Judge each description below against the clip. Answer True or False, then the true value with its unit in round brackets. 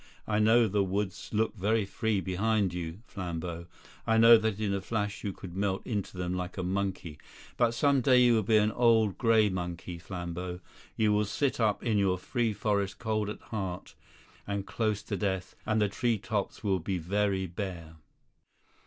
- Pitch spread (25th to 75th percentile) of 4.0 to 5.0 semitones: False (3.0 semitones)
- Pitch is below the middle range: True (100 Hz)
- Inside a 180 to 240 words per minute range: True (185 wpm)